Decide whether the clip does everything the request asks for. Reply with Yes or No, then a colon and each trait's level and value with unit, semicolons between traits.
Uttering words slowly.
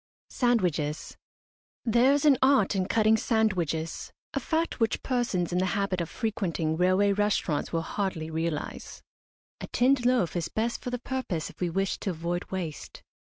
No: average, 160 wpm